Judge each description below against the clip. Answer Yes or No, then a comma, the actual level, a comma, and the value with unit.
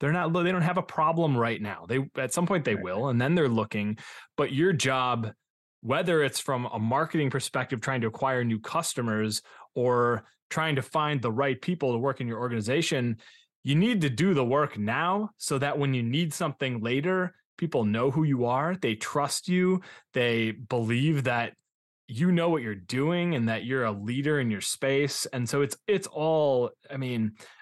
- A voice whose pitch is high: No, low, 135 Hz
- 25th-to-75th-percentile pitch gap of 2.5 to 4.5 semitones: No, average, 5.1 semitones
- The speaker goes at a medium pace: Yes, average, 195 wpm